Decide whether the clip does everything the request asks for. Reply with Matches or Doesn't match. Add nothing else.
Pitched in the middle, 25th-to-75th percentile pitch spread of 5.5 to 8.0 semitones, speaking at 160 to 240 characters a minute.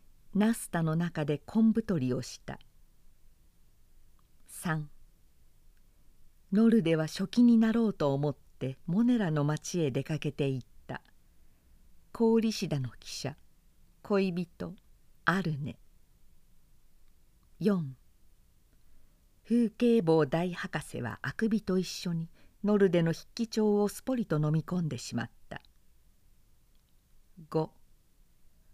Matches